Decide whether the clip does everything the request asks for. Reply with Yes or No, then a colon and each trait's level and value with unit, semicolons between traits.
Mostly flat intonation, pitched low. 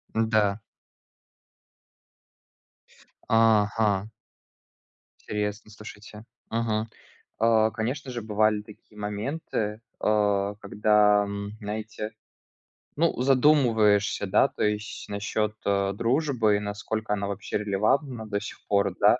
Yes: narrow, 1.5 semitones; low, 105 Hz